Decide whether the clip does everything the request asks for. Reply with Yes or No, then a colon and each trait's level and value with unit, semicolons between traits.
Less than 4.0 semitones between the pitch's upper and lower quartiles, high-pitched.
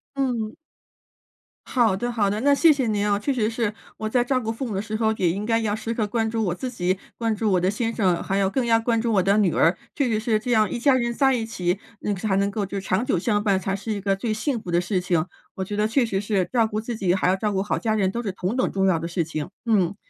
Yes: average, 3.2 semitones; high, 215 Hz